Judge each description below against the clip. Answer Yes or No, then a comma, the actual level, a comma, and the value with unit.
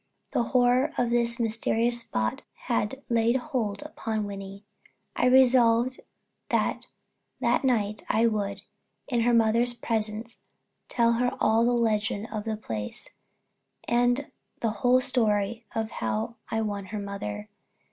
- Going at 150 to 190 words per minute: No, slow, 135 wpm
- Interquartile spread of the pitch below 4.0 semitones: Yes, narrow, 2.4 semitones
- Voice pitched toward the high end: Yes, high, 230 Hz